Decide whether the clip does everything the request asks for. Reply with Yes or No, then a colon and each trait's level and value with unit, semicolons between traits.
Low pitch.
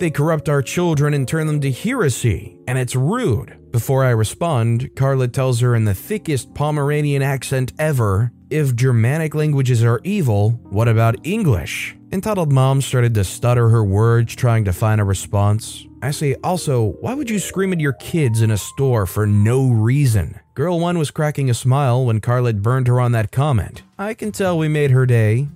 Yes: low, 130 Hz